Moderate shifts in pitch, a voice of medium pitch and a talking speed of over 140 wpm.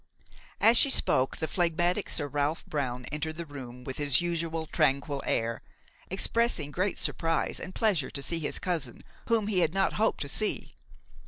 Yes: average, 4.3 semitones; medium, 160 Hz; average, 170 wpm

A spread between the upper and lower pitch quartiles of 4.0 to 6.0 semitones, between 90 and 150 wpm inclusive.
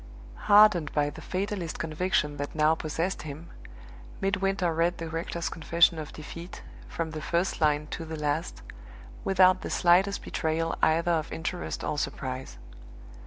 No: average, 2.7 semitones; average, 145 wpm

